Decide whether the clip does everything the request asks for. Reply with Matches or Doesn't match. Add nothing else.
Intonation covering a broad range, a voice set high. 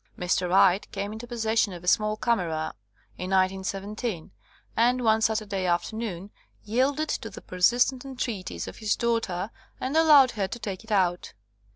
Doesn't match